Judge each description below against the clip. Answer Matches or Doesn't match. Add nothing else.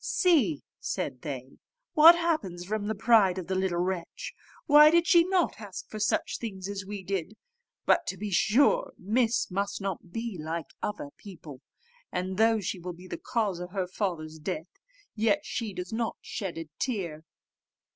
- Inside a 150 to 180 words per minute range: Matches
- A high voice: Matches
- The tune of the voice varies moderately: Matches